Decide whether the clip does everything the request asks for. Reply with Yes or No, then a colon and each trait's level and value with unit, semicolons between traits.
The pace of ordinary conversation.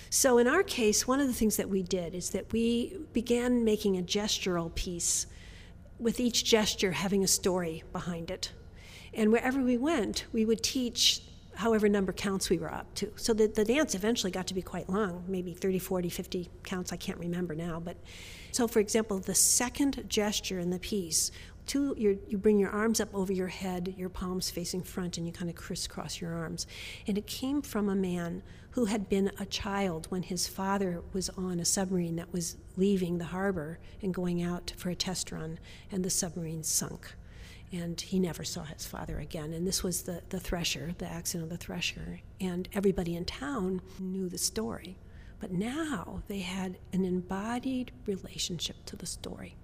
Yes: average, 195 wpm